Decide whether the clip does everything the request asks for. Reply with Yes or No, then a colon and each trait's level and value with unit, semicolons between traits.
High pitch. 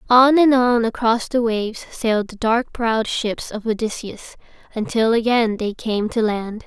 Yes: high, 225 Hz